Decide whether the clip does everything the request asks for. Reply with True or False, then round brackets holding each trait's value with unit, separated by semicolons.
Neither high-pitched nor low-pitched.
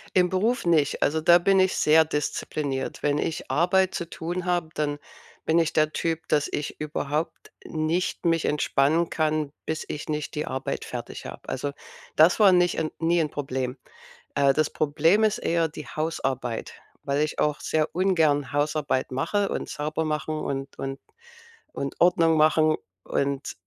True (155 Hz)